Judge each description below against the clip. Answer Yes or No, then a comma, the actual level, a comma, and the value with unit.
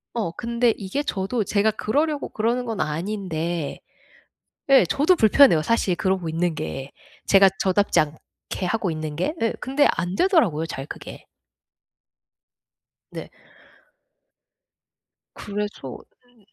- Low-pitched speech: No, high, 200 Hz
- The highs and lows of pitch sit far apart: Yes, wide, 5.9 semitones